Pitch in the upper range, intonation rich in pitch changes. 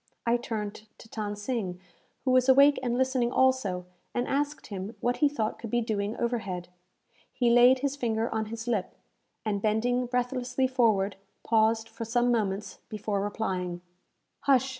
No: high, 230 Hz; average, 3.1 semitones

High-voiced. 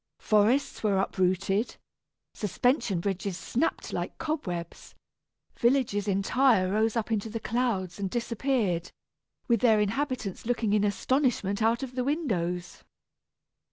Yes: high, 215 Hz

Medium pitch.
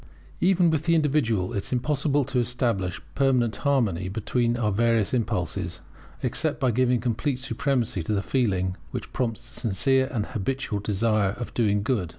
No: low, 120 Hz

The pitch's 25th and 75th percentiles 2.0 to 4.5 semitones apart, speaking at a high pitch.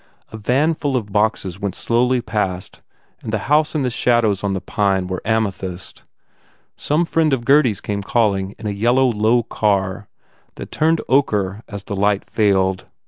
No: average, 4.1 semitones; low, 105 Hz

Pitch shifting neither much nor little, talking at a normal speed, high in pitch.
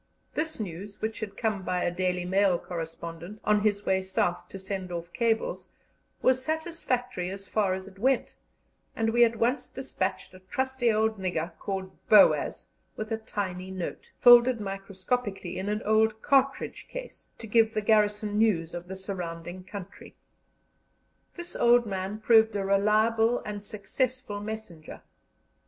Yes: average, 3.1 semitones; average, 150 wpm; high, 205 Hz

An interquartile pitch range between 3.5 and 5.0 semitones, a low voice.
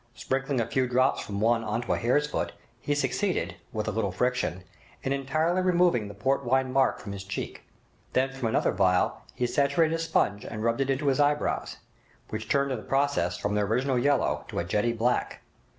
Yes: average, 4.0 semitones; low, 130 Hz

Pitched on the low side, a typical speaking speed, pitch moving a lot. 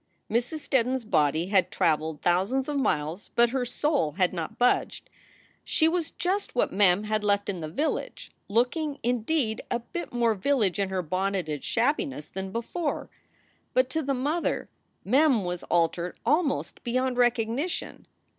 No: high, 235 Hz; average, 155 wpm; wide, 6.5 semitones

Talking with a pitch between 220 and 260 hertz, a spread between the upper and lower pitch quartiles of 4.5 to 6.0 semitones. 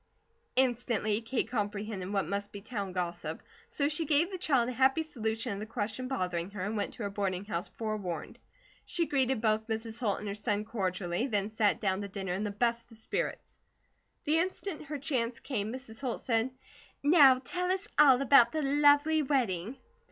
Yes: high, 225 Hz; average, 5.1 semitones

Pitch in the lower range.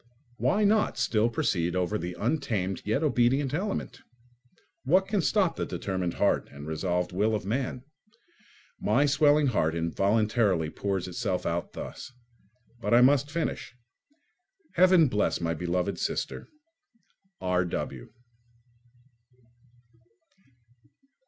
Yes: low, 110 Hz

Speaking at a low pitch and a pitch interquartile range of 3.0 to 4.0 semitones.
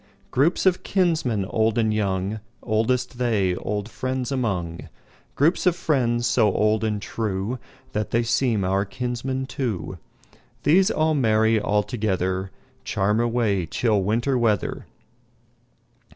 Yes: low, 110 Hz; average, 3.6 semitones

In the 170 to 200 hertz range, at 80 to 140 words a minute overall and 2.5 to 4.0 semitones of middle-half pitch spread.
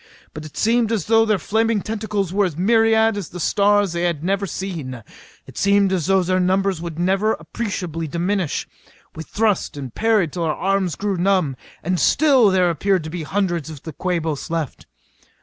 No: high, 190 Hz; average, 185 wpm; average, 3.6 semitones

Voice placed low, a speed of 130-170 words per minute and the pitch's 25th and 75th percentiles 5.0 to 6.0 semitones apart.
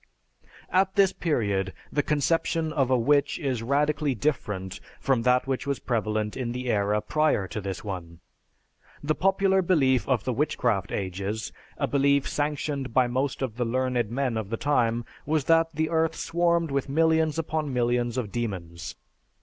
Yes: low, 130 Hz; average, 165 wpm; average, 5.3 semitones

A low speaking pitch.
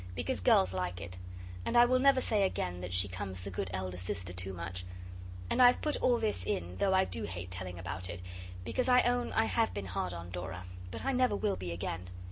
Yes: very low, 95 Hz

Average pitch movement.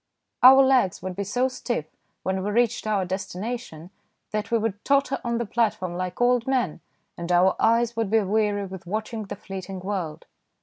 Yes: average, 4.0 semitones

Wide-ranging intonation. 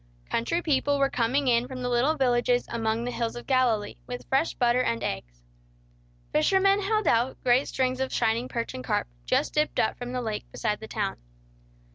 No: narrow, 2.6 semitones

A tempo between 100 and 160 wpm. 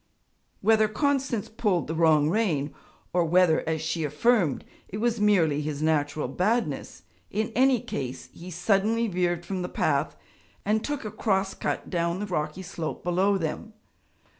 Yes: average, 155 wpm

